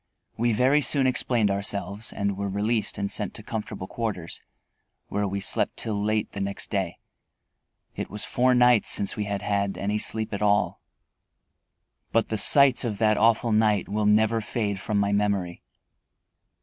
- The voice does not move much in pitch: Yes, narrow, 2.0 semitones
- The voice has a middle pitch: No, low, 105 Hz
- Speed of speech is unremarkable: Yes, average, 165 wpm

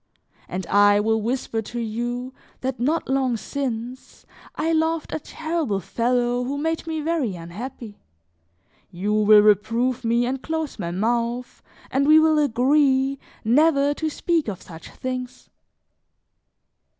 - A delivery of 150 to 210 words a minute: No, slow, 135 wpm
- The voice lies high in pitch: Yes, very high, 250 Hz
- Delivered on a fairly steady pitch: No, average, 4.6 semitones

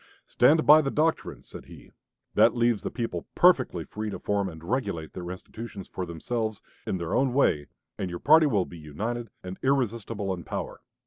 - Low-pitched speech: Yes, low, 105 Hz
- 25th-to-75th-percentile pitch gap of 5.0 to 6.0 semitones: Yes, wide, 5.6 semitones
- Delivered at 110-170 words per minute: No, average, 185 wpm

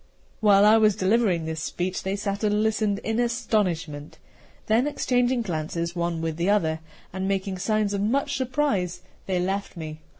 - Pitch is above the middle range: Yes, high, 200 Hz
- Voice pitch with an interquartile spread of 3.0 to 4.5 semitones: Yes, average, 4.1 semitones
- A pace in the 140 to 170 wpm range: Yes, average, 165 wpm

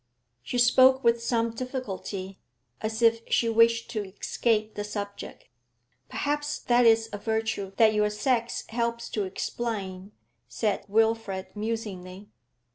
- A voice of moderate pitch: No, high, 225 Hz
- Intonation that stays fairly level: Yes, narrow, 2.2 semitones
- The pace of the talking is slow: Yes, slow, 125 wpm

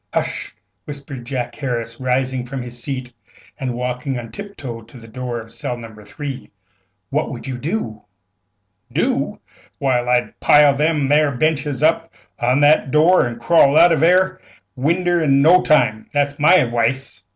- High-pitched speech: No, low, 135 Hz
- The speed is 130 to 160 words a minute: No, average, 170 wpm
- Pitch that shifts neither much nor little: Yes, average, 3.8 semitones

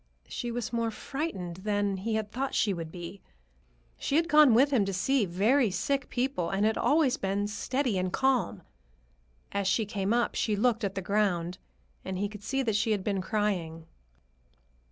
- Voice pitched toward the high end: Yes, high, 210 Hz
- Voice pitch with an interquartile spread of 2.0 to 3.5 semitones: No, average, 4.3 semitones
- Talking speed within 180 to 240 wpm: Yes, average, 185 wpm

